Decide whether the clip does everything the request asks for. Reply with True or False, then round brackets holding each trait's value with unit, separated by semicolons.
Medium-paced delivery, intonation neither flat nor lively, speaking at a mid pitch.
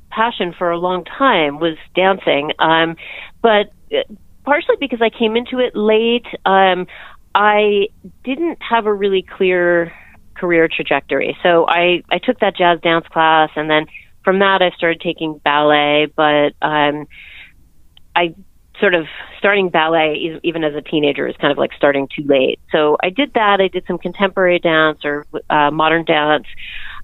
True (160 wpm; 4.6 semitones; 175 Hz)